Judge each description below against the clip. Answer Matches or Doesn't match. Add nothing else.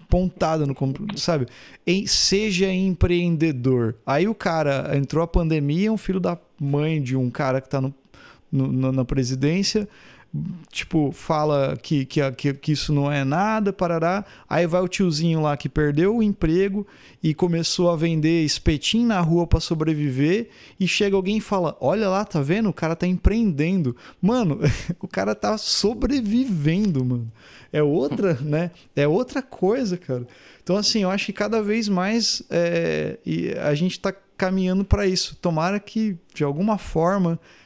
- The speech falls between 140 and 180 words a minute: Matches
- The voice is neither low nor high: Matches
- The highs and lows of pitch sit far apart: Doesn't match